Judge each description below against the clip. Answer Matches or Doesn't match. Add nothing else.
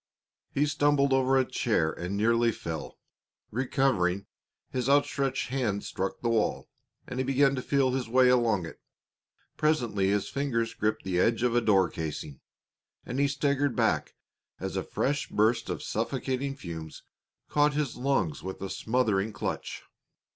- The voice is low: Matches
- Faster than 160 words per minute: Doesn't match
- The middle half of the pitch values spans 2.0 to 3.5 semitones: Doesn't match